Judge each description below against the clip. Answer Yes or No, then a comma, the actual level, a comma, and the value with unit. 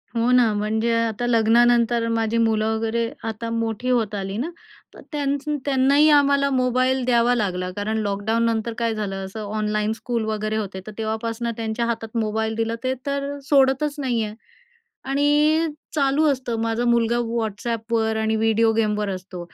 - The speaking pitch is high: Yes, high, 230 Hz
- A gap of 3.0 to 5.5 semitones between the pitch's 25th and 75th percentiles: No, narrow, 2.4 semitones